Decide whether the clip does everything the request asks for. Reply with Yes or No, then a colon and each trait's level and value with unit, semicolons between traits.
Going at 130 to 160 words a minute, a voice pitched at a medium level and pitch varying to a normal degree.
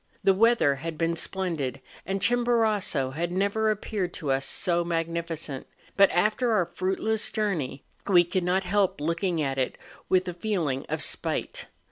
Yes: average, 155 wpm; medium, 180 Hz; average, 3.7 semitones